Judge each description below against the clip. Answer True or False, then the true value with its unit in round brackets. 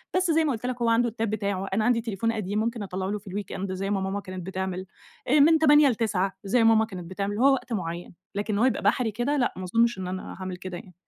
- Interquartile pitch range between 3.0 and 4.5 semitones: True (3.9 semitones)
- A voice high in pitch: True (210 Hz)